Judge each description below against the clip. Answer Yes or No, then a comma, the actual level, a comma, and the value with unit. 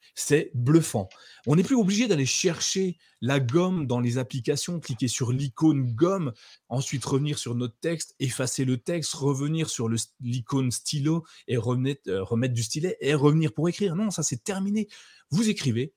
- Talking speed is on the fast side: No, average, 175 wpm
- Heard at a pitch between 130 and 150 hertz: Yes, medium, 140 Hz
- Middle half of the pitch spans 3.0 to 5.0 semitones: Yes, average, 4.7 semitones